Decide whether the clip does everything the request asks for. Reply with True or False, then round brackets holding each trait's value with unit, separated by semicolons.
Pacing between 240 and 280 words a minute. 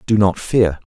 False (200 wpm)